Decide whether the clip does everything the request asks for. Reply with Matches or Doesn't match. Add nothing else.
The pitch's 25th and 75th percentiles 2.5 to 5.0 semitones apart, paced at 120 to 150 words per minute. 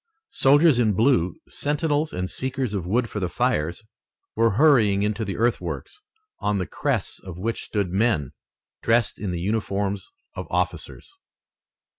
Matches